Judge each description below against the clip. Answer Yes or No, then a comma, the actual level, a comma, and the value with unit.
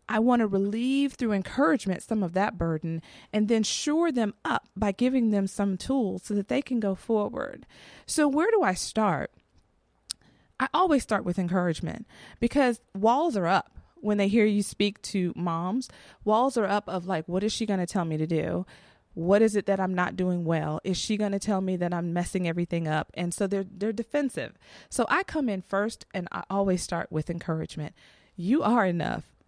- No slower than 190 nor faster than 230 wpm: Yes, average, 200 wpm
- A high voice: Yes, high, 200 Hz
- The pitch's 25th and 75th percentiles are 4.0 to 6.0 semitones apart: Yes, average, 4.3 semitones